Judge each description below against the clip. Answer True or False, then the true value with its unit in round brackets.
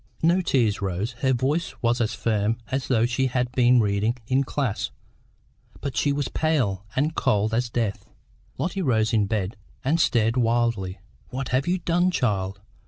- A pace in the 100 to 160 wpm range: False (170 wpm)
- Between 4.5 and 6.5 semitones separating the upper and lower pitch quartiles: False (4.0 semitones)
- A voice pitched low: True (120 Hz)